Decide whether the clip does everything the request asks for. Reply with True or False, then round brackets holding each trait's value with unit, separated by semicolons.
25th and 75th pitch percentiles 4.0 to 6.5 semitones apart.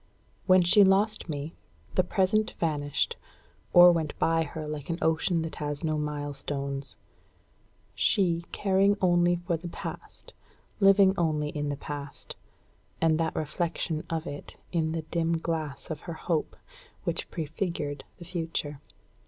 False (2.8 semitones)